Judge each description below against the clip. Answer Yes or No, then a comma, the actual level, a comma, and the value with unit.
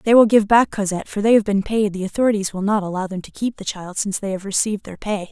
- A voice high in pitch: Yes, high, 205 Hz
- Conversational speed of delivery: No, fast, 295 wpm